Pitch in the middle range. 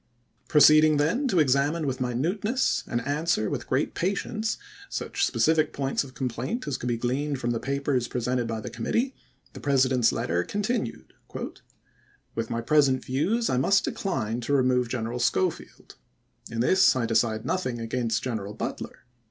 No: low, 130 Hz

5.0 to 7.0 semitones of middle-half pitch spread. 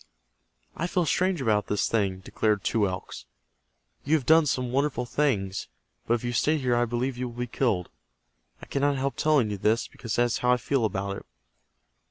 No: average, 4.4 semitones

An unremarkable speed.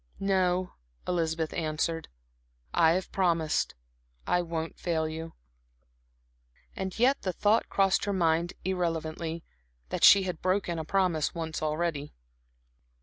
No: slow, 120 wpm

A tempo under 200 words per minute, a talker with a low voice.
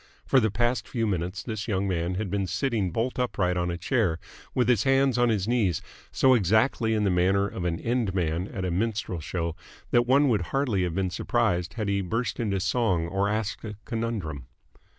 No: fast, 205 wpm; low, 100 Hz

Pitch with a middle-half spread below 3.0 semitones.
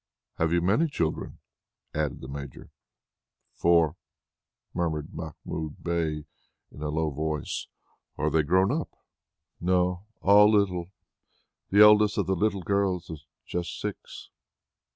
No: average, 3.8 semitones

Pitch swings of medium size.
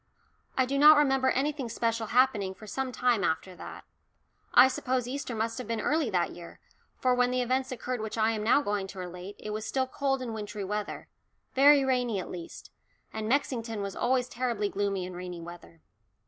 Yes: average, 4.2 semitones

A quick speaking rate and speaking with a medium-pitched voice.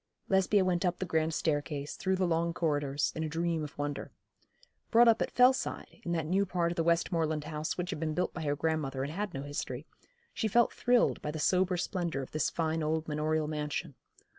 Yes: fast, 215 wpm; medium, 160 Hz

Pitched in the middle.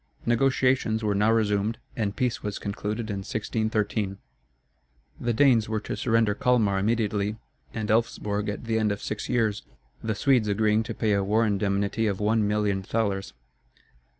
No: low, 105 Hz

